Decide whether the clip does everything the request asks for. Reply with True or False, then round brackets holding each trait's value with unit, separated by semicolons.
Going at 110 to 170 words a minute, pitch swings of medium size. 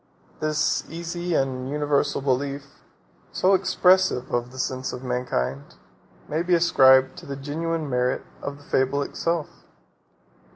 True (135 wpm; 4.1 semitones)